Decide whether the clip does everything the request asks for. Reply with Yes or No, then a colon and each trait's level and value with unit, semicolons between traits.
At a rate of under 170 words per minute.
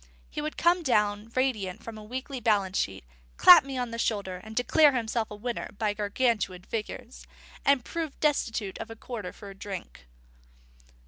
No: average, 175 wpm